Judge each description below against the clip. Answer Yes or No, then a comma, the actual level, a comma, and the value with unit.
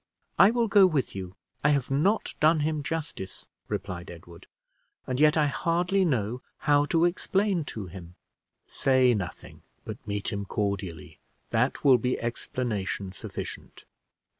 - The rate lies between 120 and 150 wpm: Yes, average, 140 wpm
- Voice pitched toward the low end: Yes, low, 130 Hz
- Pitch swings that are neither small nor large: No, wide, 8.0 semitones